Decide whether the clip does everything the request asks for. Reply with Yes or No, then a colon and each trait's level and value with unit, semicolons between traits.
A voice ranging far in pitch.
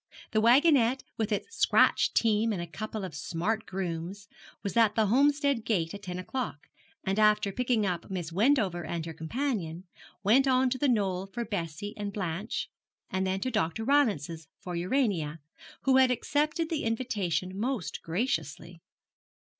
Yes: wide, 5.8 semitones